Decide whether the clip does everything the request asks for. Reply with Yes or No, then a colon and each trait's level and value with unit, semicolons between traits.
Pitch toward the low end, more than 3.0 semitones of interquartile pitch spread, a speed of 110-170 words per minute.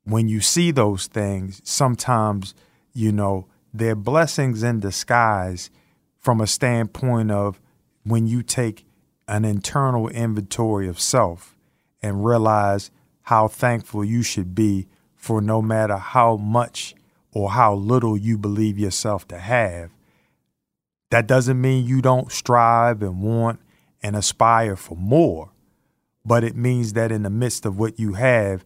No: low, 110 Hz; average, 2.7 semitones; average, 140 wpm